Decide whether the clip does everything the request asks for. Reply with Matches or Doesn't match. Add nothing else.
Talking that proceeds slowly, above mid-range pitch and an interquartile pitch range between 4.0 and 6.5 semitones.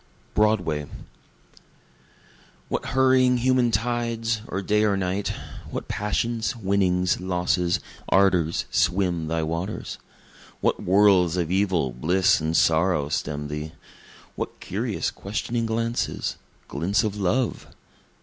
Doesn't match